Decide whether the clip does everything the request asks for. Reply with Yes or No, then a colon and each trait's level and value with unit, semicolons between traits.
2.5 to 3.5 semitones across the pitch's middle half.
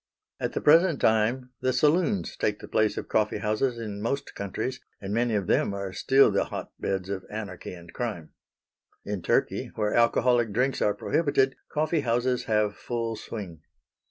No: average, 3.9 semitones